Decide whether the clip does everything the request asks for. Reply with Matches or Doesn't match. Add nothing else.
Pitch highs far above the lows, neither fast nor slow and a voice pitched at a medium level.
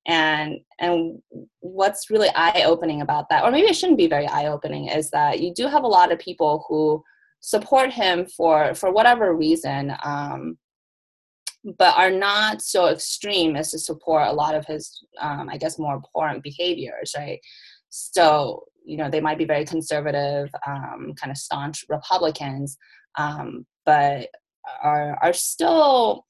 Doesn't match